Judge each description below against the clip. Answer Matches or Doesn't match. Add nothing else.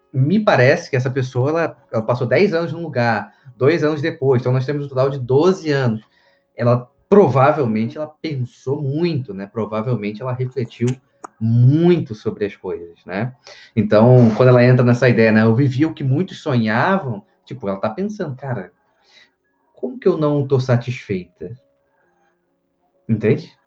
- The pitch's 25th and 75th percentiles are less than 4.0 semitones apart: Doesn't match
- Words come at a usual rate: Matches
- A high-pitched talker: Doesn't match